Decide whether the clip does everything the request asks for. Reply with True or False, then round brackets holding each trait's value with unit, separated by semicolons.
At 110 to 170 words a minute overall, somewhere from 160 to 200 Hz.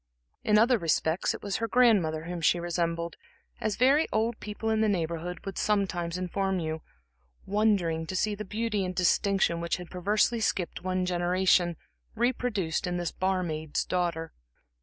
True (160 wpm; 185 Hz)